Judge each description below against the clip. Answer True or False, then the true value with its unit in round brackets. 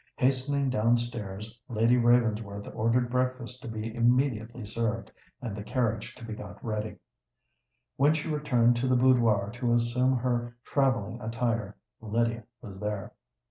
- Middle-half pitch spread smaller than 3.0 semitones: True (2.5 semitones)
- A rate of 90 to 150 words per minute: True (140 wpm)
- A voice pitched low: True (120 Hz)